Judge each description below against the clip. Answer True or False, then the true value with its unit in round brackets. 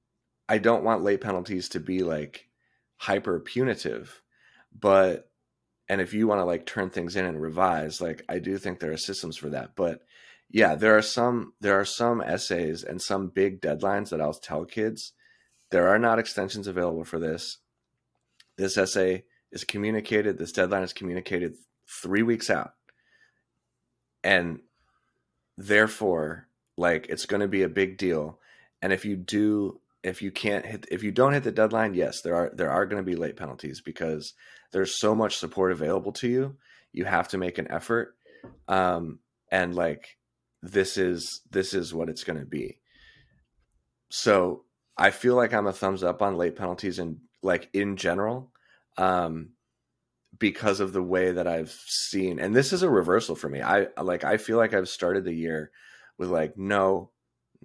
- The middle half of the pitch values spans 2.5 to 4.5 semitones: True (3.2 semitones)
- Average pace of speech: True (175 wpm)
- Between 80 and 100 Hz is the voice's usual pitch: True (95 Hz)